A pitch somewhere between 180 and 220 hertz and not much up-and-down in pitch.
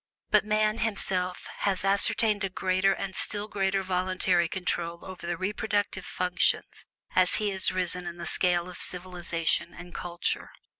Yes: medium, 185 Hz; narrow, 1.7 semitones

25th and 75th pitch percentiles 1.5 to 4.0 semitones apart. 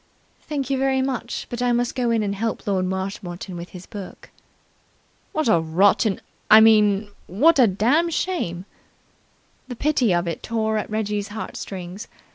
No: average, 4.5 semitones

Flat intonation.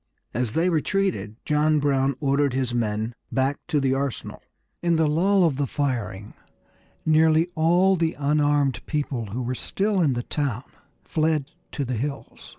No: average, 3.8 semitones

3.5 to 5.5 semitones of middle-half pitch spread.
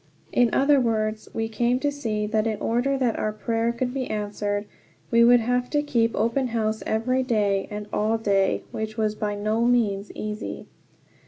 No: narrow, 2.4 semitones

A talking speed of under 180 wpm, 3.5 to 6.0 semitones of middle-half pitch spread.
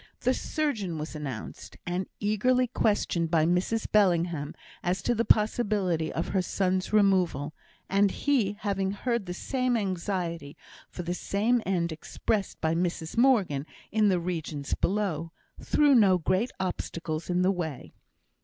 Yes: average, 145 wpm; average, 4.0 semitones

